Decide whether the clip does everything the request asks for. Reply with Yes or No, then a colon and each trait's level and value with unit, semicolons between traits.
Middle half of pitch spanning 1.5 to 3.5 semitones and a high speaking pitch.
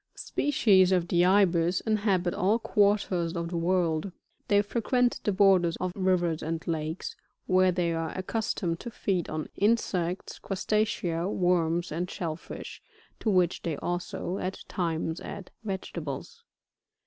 No: average, 2.7 semitones; medium, 180 Hz